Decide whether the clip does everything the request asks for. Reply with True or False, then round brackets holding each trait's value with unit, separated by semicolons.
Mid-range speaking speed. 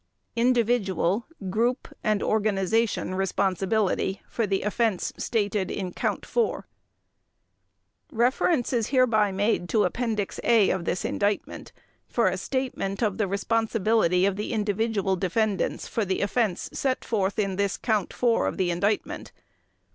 False (130 wpm)